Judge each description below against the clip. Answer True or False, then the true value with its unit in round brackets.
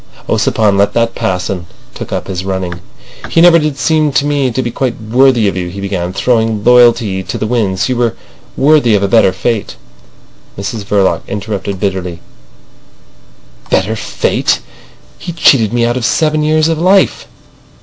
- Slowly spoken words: False (170 wpm)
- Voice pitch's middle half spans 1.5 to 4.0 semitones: False (5.3 semitones)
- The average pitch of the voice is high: False (110 Hz)